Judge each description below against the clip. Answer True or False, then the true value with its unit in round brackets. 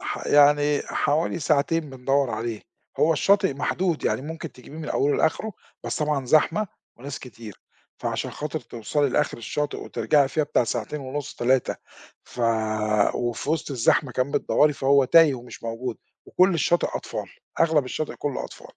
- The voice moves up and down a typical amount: True (3.3 semitones)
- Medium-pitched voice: True (145 Hz)